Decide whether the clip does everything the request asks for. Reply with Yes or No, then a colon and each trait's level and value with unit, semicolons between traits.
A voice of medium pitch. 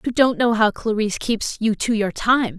No: high, 225 Hz